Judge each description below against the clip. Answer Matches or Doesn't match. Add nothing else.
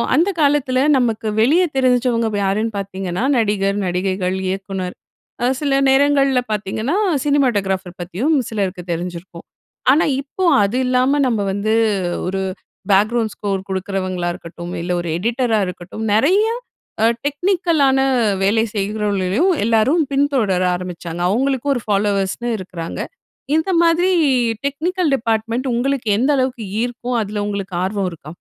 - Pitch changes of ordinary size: Doesn't match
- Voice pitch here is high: Matches